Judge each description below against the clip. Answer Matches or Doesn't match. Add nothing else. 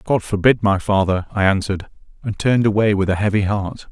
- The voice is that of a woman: Doesn't match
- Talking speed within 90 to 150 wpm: Doesn't match